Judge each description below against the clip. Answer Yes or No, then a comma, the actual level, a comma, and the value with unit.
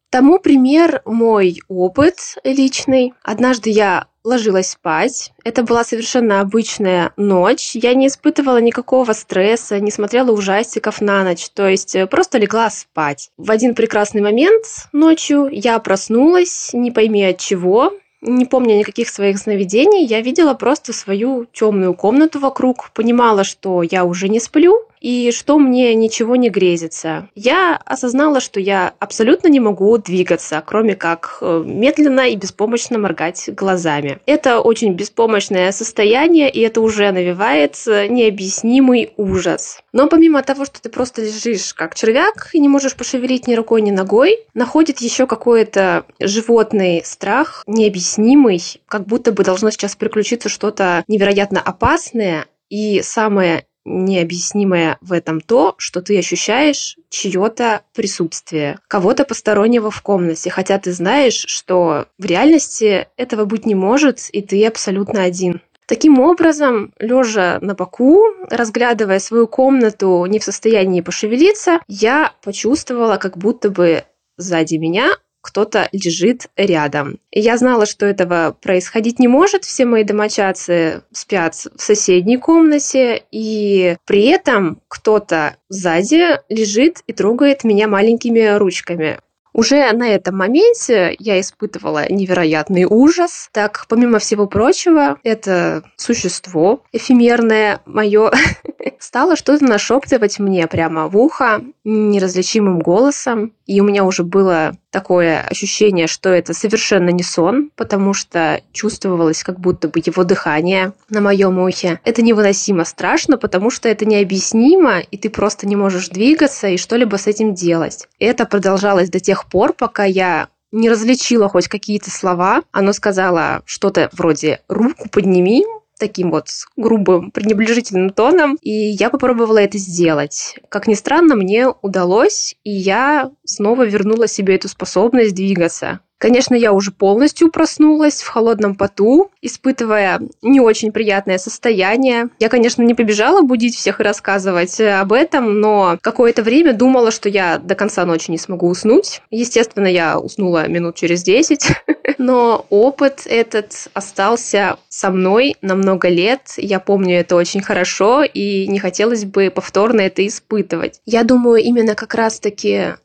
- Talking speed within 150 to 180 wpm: No, average, 135 wpm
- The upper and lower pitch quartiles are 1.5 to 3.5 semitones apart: No, average, 4.5 semitones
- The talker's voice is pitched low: No, high, 215 Hz